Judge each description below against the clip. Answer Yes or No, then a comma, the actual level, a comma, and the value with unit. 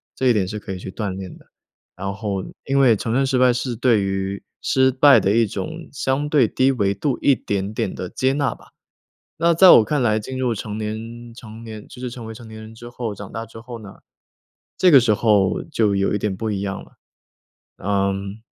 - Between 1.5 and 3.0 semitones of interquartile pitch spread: No, average, 4.0 semitones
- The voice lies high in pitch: No, low, 110 Hz